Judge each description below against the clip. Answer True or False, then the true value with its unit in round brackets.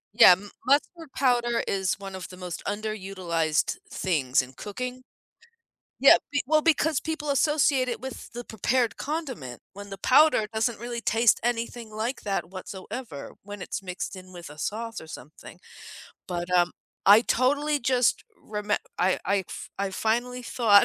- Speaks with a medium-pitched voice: False (220 Hz)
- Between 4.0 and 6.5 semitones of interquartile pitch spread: True (5.2 semitones)